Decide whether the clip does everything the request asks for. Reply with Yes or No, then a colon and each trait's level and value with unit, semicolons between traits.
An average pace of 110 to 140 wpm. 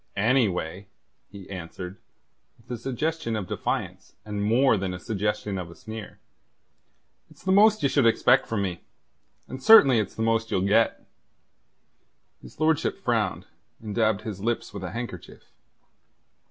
No: average, 150 wpm